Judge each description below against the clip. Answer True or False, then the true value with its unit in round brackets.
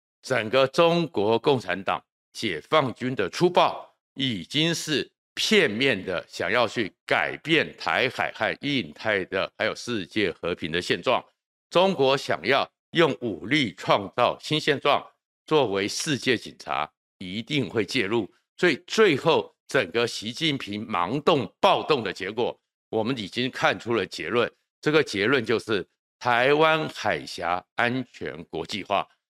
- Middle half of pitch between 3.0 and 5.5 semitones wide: True (5.2 semitones)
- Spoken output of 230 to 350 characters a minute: False (205 characters per minute)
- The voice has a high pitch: False (135 Hz)